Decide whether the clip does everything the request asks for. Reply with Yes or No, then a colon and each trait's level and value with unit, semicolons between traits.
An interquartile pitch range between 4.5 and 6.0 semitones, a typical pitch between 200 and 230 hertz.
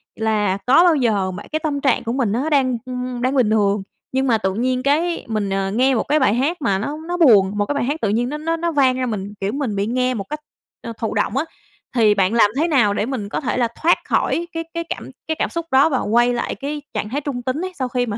No: average, 5.2 semitones; very high, 250 Hz